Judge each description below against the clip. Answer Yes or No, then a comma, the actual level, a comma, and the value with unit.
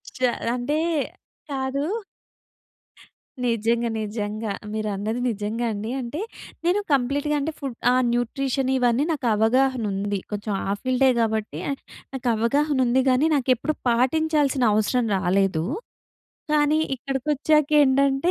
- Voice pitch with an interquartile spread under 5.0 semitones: Yes, average, 4.1 semitones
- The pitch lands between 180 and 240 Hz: No, very high, 255 Hz